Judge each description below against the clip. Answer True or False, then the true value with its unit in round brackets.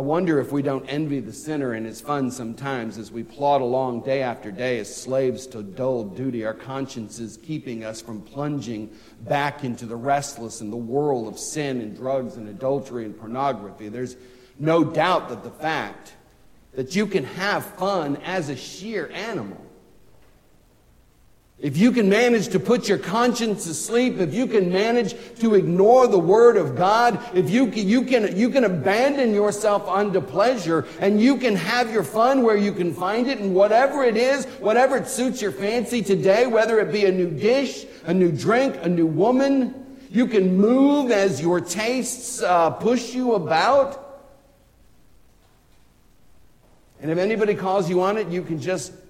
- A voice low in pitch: False (185 Hz)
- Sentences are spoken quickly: False (175 wpm)